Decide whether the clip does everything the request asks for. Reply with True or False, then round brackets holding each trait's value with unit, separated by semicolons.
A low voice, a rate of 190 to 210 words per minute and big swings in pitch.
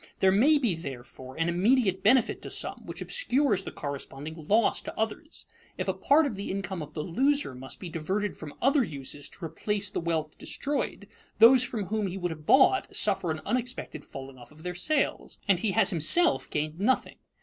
False (190 Hz; 195 wpm; 7.5 semitones)